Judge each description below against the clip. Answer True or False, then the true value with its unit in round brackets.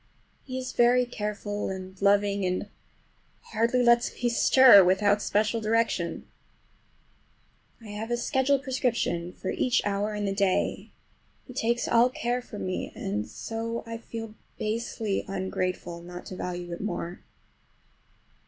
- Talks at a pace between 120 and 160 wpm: True (135 wpm)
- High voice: True (210 Hz)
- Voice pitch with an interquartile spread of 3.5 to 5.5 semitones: True (4.0 semitones)